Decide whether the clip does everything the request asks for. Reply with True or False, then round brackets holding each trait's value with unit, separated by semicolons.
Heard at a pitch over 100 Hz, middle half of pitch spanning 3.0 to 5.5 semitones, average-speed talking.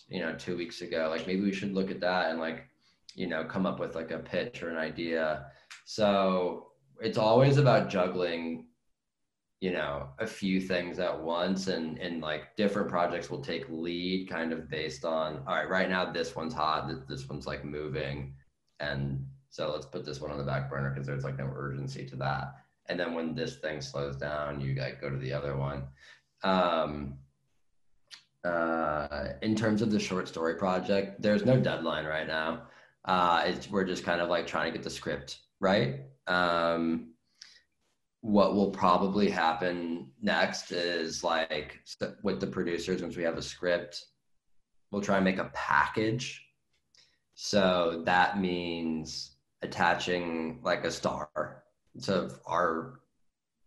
False (85 Hz; 4.0 semitones; 170 wpm)